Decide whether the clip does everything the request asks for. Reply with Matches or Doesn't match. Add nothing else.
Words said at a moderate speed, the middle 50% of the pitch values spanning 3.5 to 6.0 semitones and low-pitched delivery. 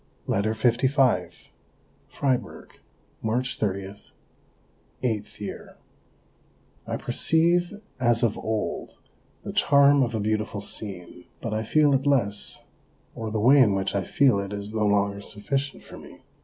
Doesn't match